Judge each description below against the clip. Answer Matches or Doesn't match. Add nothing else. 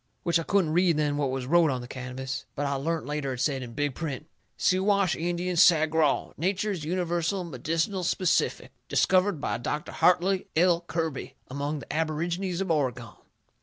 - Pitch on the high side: Doesn't match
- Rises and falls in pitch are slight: Doesn't match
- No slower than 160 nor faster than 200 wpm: Matches